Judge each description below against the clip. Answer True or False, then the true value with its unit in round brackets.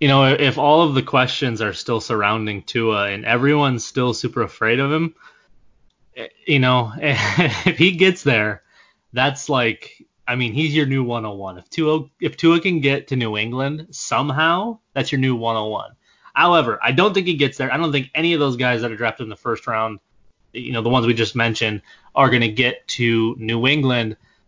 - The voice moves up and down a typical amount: True (4.2 semitones)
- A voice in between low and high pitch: False (130 Hz)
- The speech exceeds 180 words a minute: True (200 wpm)